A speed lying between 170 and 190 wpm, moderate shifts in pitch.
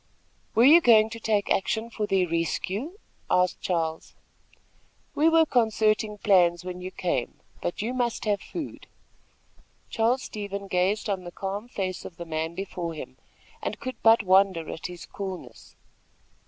No: average, 155 wpm; average, 4.0 semitones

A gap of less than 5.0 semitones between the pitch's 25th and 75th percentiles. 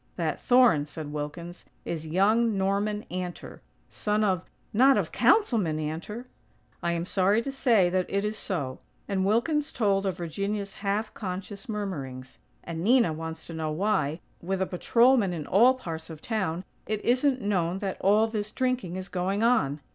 Yes: average, 4.3 semitones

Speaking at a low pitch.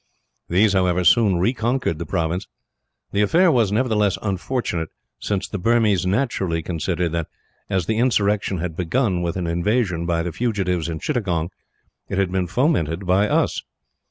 Yes: very low, 95 Hz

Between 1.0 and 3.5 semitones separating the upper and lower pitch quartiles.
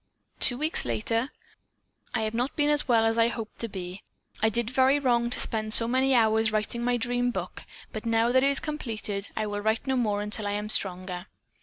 Yes: narrow, 2.6 semitones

